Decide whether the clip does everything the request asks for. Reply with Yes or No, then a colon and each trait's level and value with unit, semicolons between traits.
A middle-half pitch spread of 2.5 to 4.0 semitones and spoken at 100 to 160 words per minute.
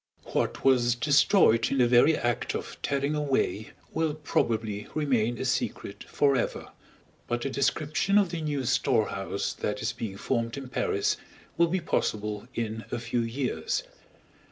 No: average, 4.6 semitones; average, 150 wpm